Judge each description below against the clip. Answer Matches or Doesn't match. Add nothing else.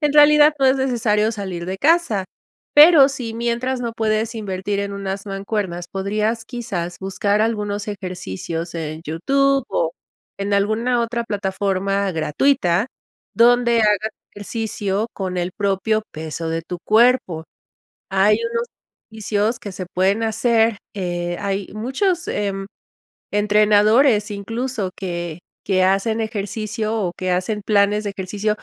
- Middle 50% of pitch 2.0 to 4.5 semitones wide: Matches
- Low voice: Doesn't match